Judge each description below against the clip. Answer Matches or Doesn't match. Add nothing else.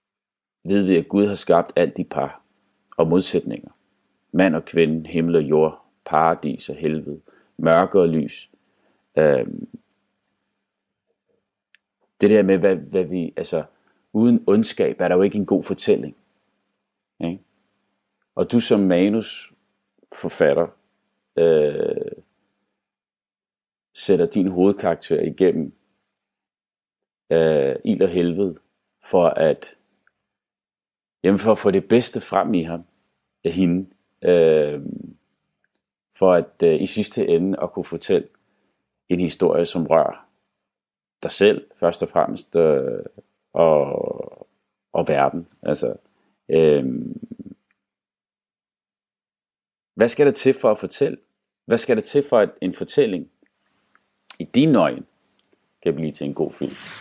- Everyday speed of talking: Doesn't match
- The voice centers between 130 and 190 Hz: Doesn't match